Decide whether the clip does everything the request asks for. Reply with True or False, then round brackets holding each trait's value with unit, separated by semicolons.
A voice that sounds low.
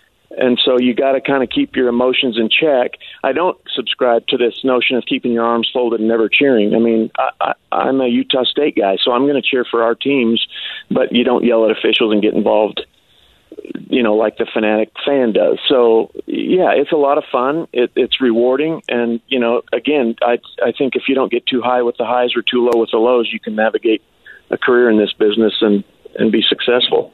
True (120 Hz)